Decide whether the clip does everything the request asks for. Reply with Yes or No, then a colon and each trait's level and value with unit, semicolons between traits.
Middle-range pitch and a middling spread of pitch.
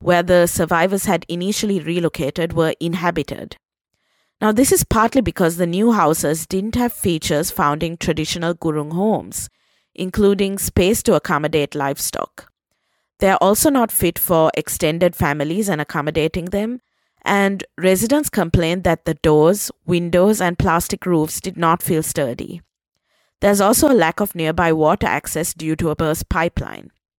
Yes: medium, 175 Hz; average, 3.8 semitones